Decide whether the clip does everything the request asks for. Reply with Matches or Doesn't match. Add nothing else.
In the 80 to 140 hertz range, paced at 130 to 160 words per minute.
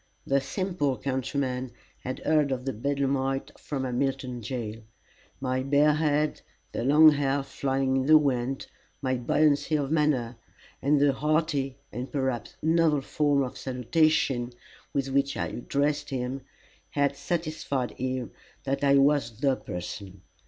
Matches